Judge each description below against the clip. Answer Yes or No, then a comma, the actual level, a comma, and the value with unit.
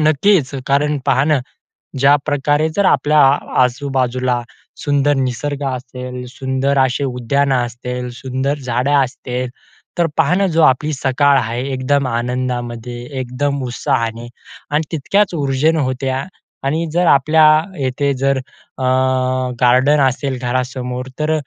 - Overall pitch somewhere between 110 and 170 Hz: Yes, low, 135 Hz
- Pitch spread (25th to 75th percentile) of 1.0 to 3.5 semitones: Yes, narrow, 2.5 semitones